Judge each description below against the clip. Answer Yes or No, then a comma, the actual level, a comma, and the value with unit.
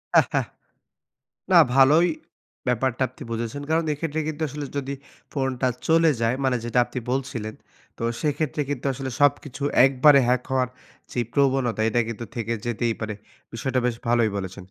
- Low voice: Yes, low, 130 Hz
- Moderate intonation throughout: Yes, average, 3.2 semitones